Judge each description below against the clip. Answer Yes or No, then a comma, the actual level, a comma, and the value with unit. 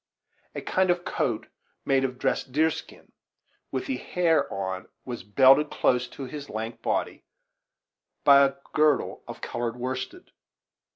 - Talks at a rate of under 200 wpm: Yes, average, 140 wpm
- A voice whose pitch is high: No, low, 135 Hz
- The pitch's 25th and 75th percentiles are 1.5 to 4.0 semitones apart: Yes, average, 3.5 semitones